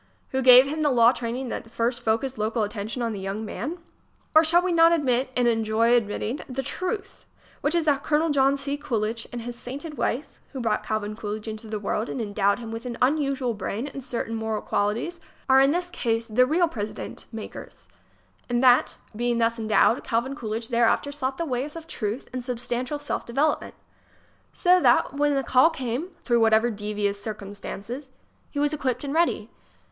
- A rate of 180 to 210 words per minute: Yes, average, 190 wpm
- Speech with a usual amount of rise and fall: Yes, average, 4.1 semitones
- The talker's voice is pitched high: Yes, high, 245 Hz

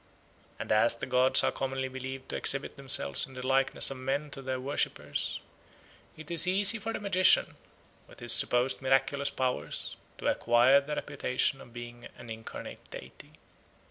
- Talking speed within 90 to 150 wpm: No, average, 165 wpm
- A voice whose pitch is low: Yes, low, 130 Hz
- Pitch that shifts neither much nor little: No, narrow, 1.9 semitones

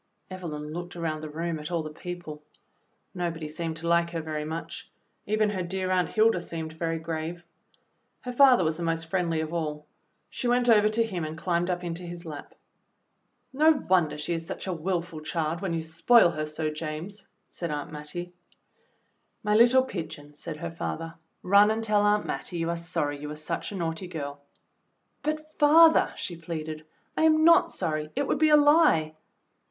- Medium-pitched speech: Yes, medium, 170 Hz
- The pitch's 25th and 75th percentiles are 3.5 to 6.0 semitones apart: Yes, average, 4.1 semitones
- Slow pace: No, average, 190 wpm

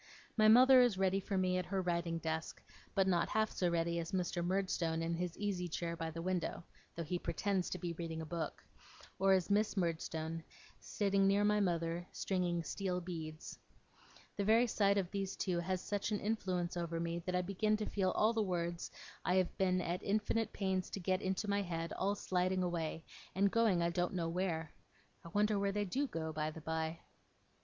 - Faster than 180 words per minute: Yes, average, 200 wpm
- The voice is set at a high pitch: No, medium, 180 Hz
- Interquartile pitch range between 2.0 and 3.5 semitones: Yes, average, 2.8 semitones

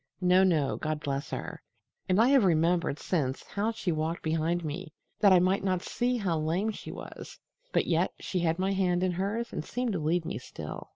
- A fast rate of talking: Yes, fast, 210 wpm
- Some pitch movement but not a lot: Yes, average, 3.7 semitones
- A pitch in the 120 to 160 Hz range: No, medium, 175 Hz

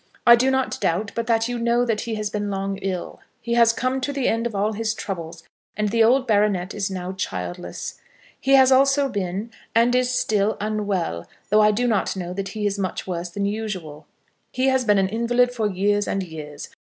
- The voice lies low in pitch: No, high, 210 Hz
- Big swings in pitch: No, average, 3.6 semitones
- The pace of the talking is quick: Yes, fast, 215 wpm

